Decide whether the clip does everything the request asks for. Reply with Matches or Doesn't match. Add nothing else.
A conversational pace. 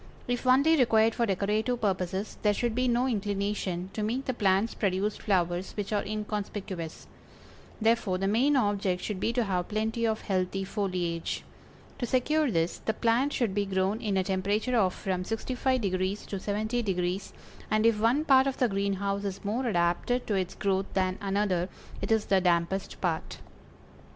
Matches